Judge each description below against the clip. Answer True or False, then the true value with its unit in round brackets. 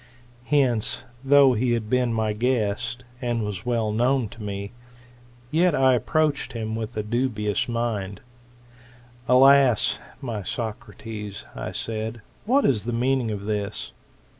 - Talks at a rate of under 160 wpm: True (140 wpm)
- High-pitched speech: False (115 Hz)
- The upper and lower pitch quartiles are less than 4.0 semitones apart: True (3.1 semitones)